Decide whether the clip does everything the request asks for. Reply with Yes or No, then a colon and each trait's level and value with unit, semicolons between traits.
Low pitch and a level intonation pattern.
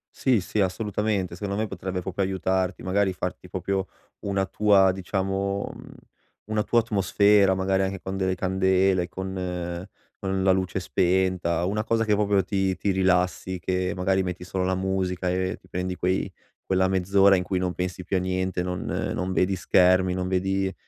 Yes: very low, 95 Hz; narrow, 1.0 semitones